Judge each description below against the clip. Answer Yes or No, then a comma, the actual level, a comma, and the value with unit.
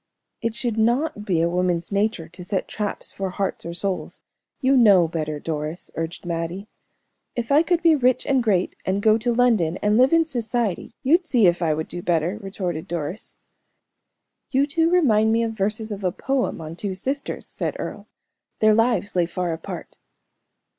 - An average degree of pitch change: No, wide, 5.7 semitones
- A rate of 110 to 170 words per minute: No, average, 180 wpm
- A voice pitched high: Yes, high, 205 Hz